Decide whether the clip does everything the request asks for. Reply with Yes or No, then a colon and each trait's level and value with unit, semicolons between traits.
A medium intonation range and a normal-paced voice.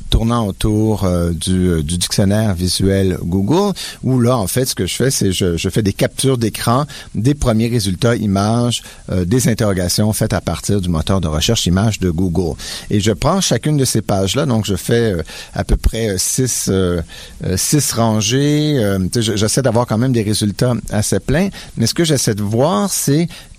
Yes: average, 4.7 semitones; average, 190 wpm